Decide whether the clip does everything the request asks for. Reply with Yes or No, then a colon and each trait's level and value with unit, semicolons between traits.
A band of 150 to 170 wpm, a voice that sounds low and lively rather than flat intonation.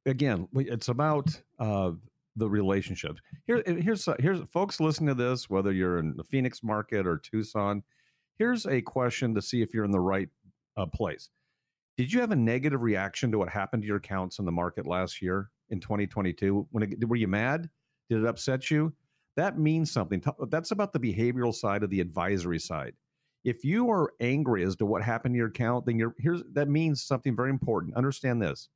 No: average, 195 wpm; low, 120 Hz; wide, 6.3 semitones